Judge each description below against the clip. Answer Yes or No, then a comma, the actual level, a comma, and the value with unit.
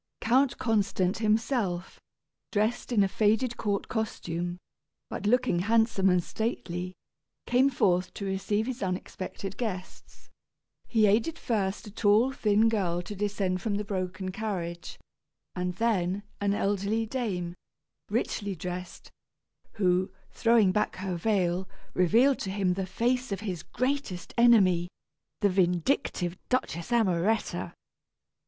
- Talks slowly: Yes, slow, 125 wpm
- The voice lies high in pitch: Yes, high, 200 Hz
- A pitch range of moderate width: Yes, average, 3.7 semitones